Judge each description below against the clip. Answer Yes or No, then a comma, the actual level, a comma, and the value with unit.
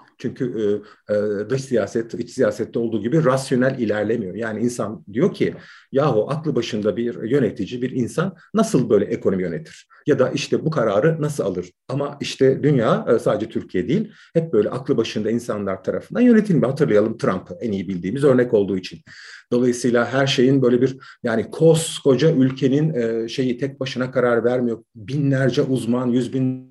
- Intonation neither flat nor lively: Yes, average, 3.4 semitones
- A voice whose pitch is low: Yes, low, 125 Hz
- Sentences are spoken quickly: Yes, fast, 165 wpm